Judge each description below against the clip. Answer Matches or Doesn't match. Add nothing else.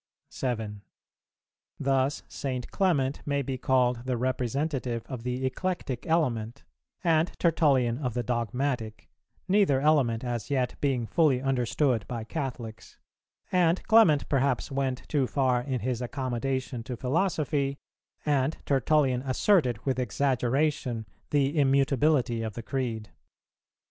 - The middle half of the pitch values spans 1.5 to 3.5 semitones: Matches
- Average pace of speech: Doesn't match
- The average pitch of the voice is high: Doesn't match